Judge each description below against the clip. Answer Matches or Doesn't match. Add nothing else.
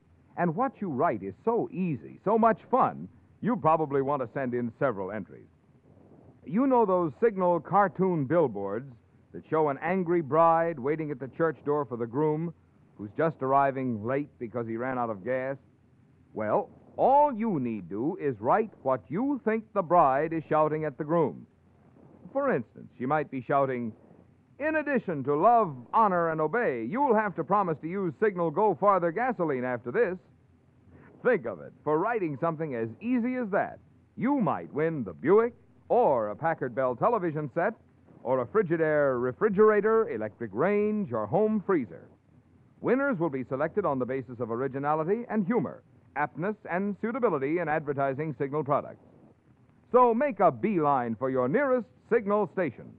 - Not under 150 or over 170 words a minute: Matches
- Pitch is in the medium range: Matches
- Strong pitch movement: Matches